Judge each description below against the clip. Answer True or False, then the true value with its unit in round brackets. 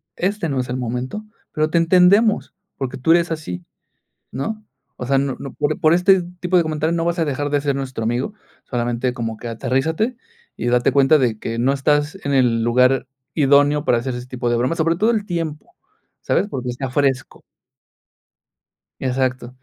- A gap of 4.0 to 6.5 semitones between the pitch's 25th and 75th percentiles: True (4.8 semitones)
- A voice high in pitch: False (140 Hz)